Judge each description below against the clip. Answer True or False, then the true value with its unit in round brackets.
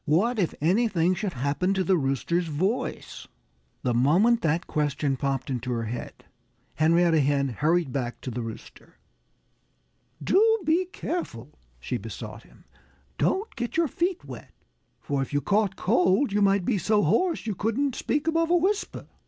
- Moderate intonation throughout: False (8.8 semitones)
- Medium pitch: True (180 Hz)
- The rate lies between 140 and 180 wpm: True (160 wpm)